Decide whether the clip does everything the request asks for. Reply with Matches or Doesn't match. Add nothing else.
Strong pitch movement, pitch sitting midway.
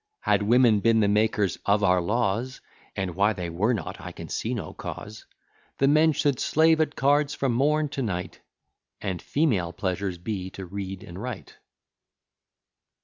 Doesn't match